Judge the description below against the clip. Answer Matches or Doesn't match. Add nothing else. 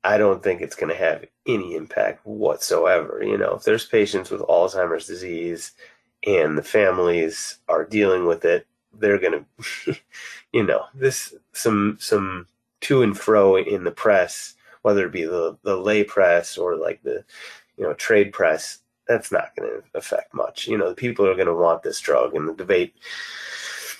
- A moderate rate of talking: Matches